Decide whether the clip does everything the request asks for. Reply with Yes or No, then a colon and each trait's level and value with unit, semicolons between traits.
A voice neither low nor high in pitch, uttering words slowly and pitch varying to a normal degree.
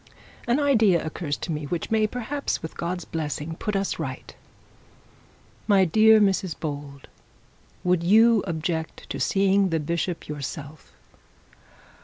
Yes: medium, 175 Hz; slow, 130 wpm; average, 5.0 semitones